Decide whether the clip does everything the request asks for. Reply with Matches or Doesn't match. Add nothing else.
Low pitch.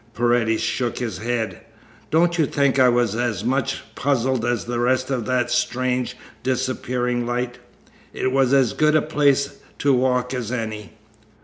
Matches